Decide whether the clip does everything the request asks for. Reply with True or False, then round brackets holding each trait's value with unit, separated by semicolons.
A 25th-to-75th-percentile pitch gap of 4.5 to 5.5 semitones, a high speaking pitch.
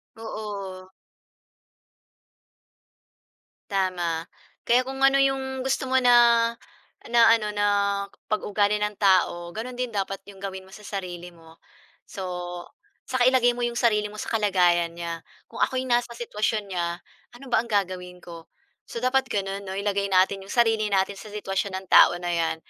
False (4.1 semitones; 205 Hz)